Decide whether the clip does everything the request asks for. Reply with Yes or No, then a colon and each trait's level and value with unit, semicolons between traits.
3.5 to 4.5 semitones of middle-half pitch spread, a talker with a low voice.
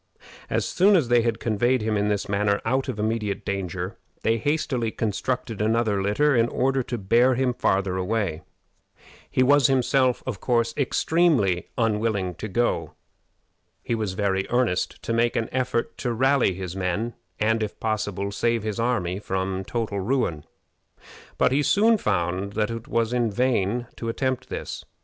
Yes: average, 3.9 semitones; low, 115 Hz